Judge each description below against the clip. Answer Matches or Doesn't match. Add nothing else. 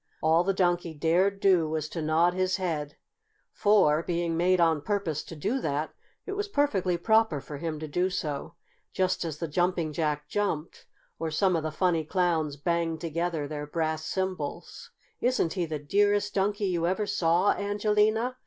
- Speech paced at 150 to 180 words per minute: Matches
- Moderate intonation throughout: Matches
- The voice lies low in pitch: Doesn't match